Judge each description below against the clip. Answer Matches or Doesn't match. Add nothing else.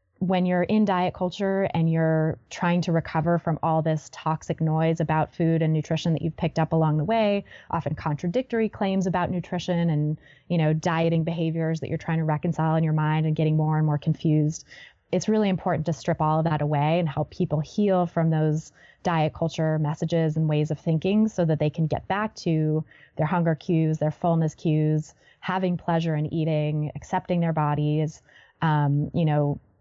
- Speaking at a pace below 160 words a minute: Doesn't match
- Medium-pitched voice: Matches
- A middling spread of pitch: Doesn't match